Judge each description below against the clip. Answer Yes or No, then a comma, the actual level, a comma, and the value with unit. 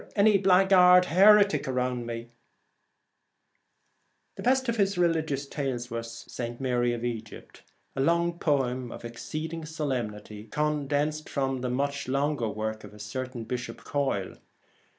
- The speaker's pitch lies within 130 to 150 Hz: Yes, low, 135 Hz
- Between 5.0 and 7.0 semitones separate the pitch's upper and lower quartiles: Yes, wide, 5.5 semitones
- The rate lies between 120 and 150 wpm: Yes, average, 140 wpm